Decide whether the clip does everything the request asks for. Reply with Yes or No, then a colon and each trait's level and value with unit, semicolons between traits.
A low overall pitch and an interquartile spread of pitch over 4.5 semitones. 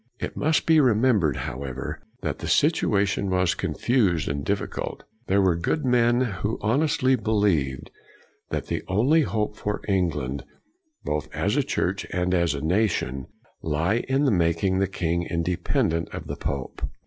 Yes: very low, 95 Hz; average, 5.3 semitones